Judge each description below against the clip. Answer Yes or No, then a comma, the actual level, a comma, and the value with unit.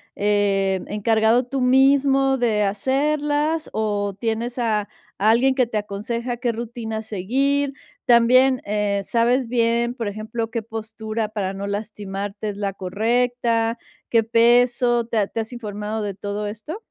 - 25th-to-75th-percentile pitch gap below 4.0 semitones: Yes, average, 2.9 semitones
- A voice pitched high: Yes, high, 225 Hz